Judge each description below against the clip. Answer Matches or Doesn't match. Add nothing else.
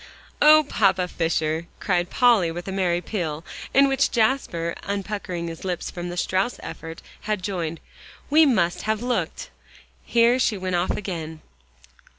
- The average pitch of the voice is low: Doesn't match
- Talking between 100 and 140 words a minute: Doesn't match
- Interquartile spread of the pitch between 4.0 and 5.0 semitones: Matches